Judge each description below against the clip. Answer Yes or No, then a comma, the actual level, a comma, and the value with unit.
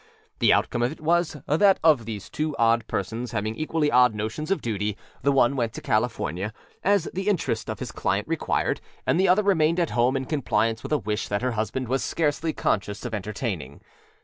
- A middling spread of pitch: No, wide, 6.3 semitones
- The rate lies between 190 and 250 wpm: Yes, average, 200 wpm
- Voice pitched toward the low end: Yes, low, 125 Hz